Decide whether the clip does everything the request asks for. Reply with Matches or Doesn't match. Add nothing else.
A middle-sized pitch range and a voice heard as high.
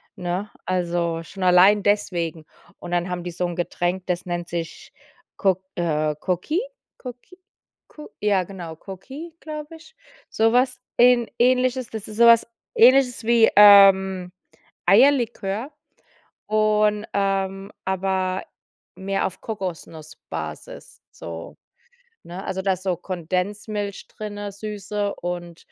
Matches